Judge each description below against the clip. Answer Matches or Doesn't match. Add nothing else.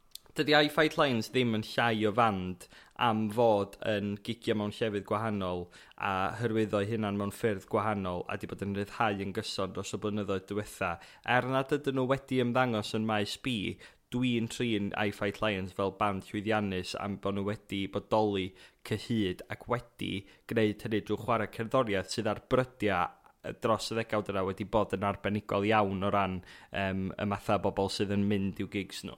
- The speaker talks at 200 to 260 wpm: Doesn't match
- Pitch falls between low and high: Doesn't match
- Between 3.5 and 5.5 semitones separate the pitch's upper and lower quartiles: Doesn't match